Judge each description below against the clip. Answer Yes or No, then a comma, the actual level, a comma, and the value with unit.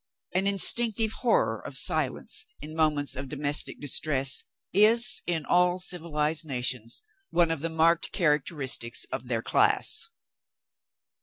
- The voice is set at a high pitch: No, medium, 160 Hz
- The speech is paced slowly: Yes, slow, 125 wpm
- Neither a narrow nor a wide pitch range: Yes, average, 4.3 semitones